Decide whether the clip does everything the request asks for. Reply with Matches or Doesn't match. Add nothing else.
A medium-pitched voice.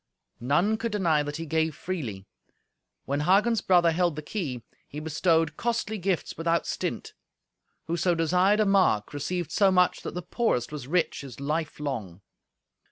Matches